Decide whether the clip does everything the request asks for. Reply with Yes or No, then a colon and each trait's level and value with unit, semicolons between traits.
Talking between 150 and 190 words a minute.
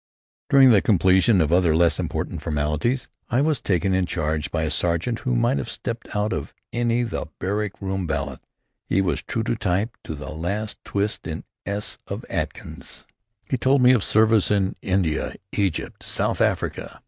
Yes: average, 185 wpm